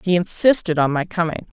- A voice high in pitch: No, medium, 175 Hz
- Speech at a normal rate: Yes, average, 190 wpm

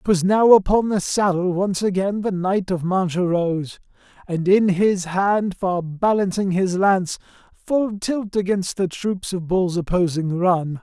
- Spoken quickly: No, average, 160 wpm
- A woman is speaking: No, male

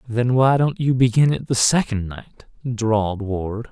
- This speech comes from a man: Yes, male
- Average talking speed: Yes, average, 180 wpm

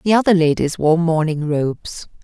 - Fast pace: No, average, 160 wpm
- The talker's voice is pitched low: No, medium, 165 Hz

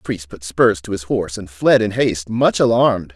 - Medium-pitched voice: No, low, 100 Hz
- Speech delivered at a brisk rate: Yes, fast, 250 wpm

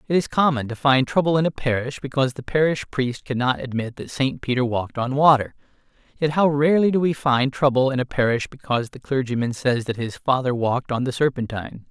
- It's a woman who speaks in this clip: No, male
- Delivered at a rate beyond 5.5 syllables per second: Yes, 5.9 syllables/s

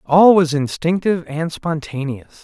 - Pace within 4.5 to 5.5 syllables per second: No, 4.3 syllables/s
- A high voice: No, medium, 160 Hz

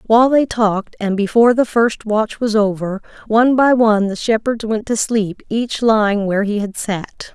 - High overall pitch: Yes, high, 220 Hz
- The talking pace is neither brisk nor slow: Yes, average, 195 wpm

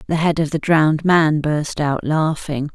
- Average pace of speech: Yes, average, 195 wpm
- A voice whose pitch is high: No, medium, 155 Hz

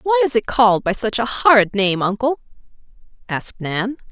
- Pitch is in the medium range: No, high, 235 Hz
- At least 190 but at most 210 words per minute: No, average, 175 wpm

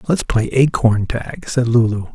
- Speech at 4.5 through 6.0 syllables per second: No, 4.3 syllables/s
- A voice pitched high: No, low, 120 Hz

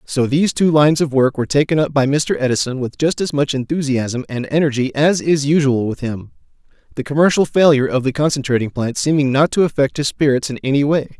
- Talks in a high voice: No, medium, 140 Hz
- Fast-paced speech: Yes, fast, 215 wpm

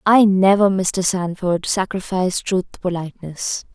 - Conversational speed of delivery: No, slow, 130 wpm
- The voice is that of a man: No, female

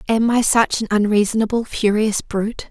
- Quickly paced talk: No, average, 155 wpm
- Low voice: No, high, 215 Hz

